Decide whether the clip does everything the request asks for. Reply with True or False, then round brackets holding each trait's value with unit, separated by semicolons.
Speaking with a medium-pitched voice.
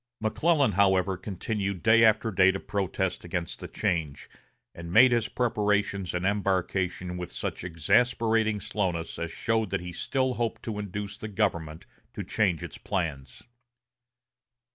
False (100 Hz)